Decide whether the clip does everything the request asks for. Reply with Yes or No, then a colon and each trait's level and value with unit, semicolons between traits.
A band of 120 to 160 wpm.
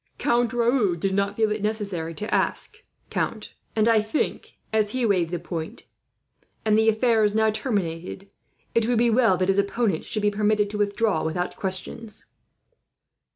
No: average, 170 wpm